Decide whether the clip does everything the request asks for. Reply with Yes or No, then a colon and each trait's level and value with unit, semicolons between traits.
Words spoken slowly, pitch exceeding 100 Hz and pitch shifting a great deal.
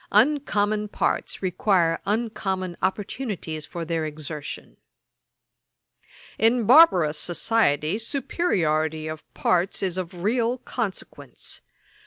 Yes: slow, 90 wpm; high, 190 Hz; wide, 5.7 semitones